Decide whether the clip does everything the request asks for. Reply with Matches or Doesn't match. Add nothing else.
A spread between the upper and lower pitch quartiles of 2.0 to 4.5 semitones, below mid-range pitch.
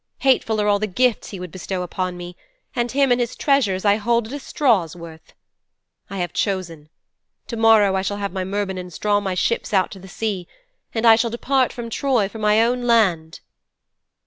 Doesn't match